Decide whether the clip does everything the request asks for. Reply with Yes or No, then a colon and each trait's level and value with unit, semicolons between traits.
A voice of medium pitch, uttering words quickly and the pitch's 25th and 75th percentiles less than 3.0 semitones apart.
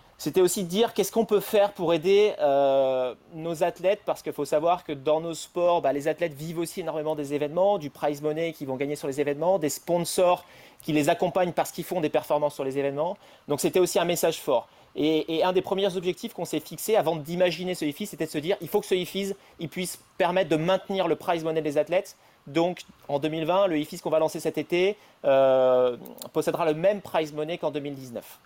No: medium, 165 Hz; fast, 225 wpm; average, 3.4 semitones